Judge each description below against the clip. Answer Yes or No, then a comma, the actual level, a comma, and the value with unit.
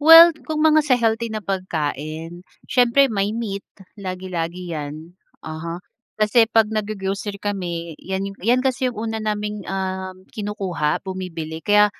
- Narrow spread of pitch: No, average, 4.2 semitones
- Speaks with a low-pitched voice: No, high, 200 Hz